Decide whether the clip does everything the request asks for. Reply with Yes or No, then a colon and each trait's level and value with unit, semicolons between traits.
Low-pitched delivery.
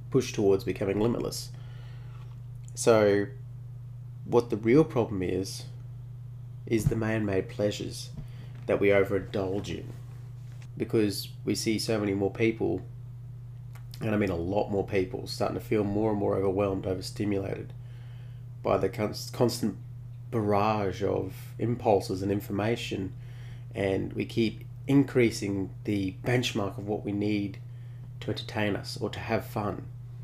Yes: low, 120 Hz